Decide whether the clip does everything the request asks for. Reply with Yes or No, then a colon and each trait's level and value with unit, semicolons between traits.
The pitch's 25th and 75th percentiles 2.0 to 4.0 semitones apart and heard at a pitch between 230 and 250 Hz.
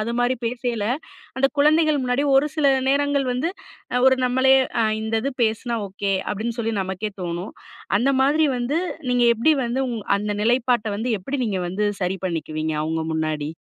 No: average, 4.9 semitones; high, 235 Hz